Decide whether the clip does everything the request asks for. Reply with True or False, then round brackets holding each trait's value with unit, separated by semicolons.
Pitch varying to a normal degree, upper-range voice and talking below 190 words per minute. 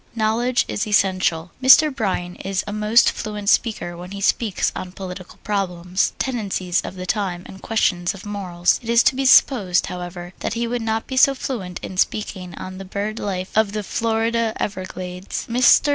True (3.6 semitones; 200 Hz; 180 wpm)